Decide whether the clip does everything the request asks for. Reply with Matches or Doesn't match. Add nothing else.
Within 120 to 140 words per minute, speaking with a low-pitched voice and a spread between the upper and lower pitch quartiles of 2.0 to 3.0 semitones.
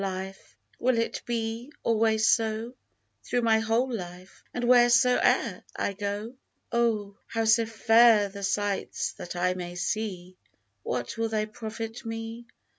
Doesn't match